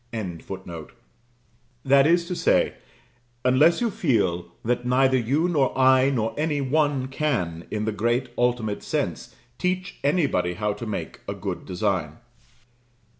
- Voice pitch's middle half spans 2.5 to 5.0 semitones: No, wide, 5.4 semitones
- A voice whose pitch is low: Yes, low, 130 Hz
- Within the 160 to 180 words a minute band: No, slow, 135 wpm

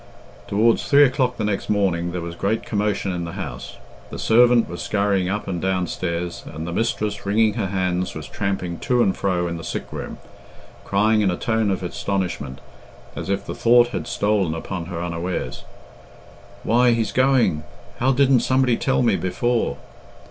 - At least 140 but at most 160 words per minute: No, average, 175 wpm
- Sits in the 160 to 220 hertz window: No, low, 100 Hz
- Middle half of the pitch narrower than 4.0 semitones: No, average, 4.5 semitones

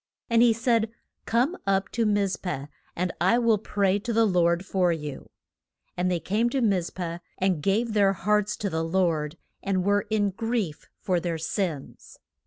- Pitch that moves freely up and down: No, average, 3.9 semitones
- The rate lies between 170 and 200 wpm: Yes, average, 180 wpm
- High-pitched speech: Yes, high, 195 Hz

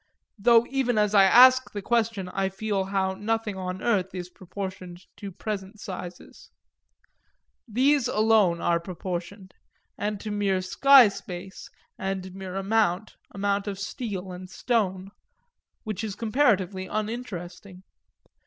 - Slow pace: Yes, slow, 125 wpm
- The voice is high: Yes, high, 195 Hz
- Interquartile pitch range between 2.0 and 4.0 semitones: Yes, narrow, 2.6 semitones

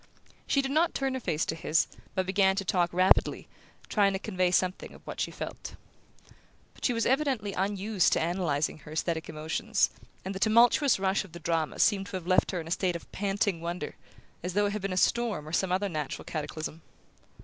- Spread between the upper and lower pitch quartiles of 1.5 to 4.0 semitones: Yes, average, 3.6 semitones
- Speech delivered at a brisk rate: Yes, fast, 210 wpm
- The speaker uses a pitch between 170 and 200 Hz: Yes, high, 190 Hz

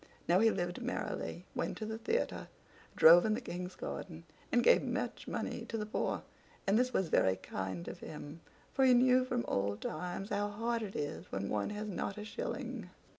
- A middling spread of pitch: No, wide, 6.0 semitones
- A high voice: Yes, high, 210 Hz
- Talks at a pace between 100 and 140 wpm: No, average, 195 wpm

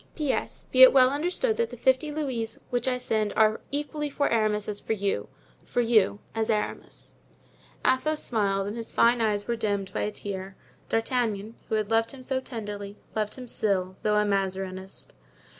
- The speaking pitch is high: Yes, high, 220 Hz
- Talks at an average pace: Yes, average, 175 wpm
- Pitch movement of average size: Yes, average, 4.0 semitones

